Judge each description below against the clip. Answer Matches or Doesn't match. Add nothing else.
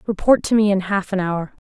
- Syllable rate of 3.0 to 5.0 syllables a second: Doesn't match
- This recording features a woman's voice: Matches